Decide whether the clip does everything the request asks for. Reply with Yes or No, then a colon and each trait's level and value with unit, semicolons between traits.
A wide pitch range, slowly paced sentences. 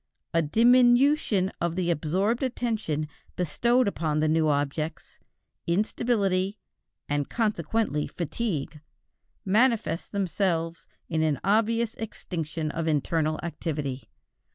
Yes: wide, 6.2 semitones; slow, 100 wpm